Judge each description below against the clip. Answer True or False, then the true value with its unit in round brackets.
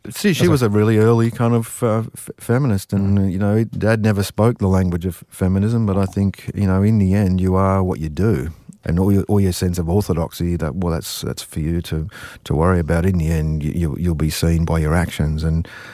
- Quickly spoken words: True (235 wpm)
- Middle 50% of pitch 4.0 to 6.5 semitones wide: True (4.4 semitones)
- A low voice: True (95 Hz)